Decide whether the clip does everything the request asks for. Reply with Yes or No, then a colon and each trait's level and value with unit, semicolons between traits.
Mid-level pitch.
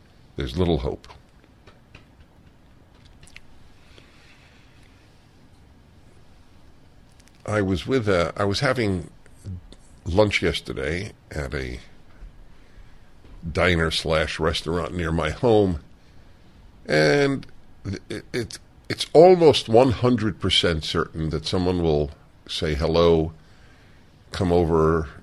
No: very low, 85 Hz